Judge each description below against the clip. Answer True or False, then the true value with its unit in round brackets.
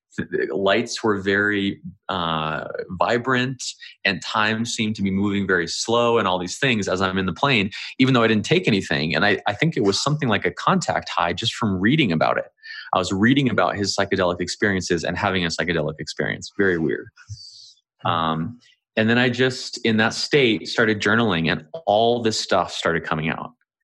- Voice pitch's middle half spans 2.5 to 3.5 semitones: False (4.0 semitones)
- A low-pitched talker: True (100 Hz)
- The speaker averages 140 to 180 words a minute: False (190 wpm)